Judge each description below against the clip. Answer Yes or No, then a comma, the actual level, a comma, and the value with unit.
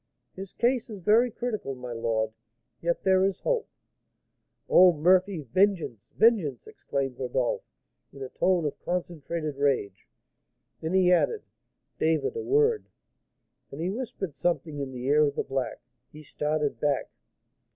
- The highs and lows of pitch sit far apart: Yes, wide, 6.0 semitones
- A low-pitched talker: No, medium, 160 Hz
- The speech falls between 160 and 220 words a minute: No, average, 145 wpm